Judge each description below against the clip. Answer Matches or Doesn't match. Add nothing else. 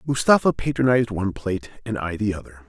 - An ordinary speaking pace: Matches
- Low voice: Matches